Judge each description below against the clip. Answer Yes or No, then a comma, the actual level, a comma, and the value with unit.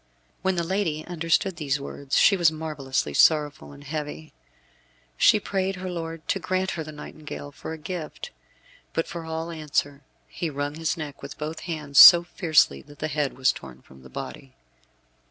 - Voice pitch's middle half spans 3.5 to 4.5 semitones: No, average, 2.9 semitones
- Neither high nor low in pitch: Yes, medium, 155 Hz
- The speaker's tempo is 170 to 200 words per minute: Yes, average, 175 wpm